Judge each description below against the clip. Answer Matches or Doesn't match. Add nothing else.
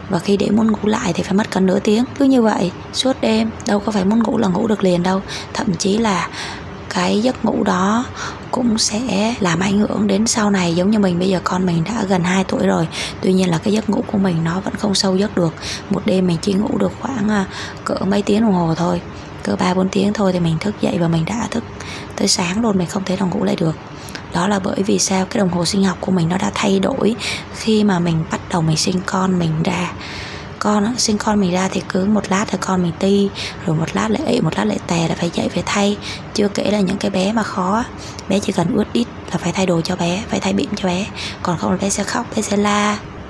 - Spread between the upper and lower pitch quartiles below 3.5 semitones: Matches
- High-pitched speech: Matches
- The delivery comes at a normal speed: Doesn't match